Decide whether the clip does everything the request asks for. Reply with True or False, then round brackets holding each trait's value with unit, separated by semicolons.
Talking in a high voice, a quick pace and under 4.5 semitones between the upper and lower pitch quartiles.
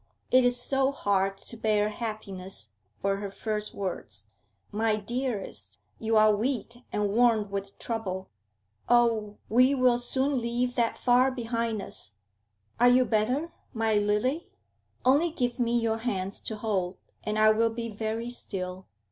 False (225 Hz; 150 wpm; 3.0 semitones)